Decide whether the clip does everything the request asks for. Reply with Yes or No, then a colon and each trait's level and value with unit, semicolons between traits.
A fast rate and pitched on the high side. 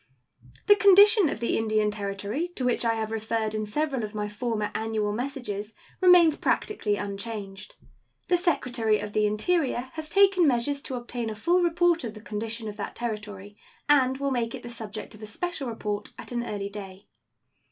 No: average, 185 wpm; high, 230 Hz